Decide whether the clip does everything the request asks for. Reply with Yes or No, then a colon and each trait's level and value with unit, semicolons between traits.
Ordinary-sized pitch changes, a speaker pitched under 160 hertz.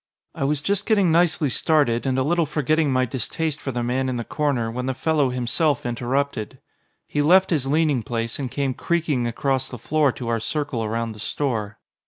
Yes: average, 4.1 semitones; low, 135 Hz